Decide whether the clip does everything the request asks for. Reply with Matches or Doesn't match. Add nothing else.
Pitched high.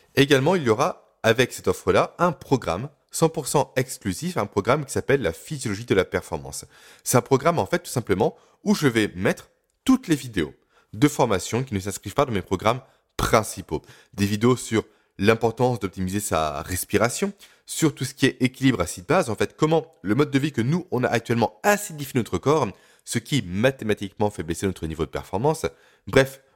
Doesn't match